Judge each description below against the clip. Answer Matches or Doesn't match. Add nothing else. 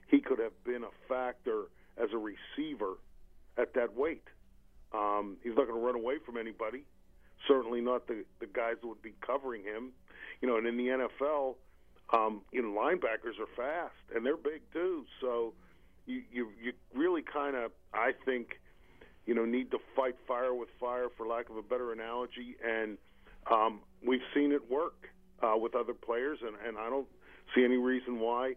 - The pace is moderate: Matches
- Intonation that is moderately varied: Doesn't match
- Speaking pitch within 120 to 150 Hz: Matches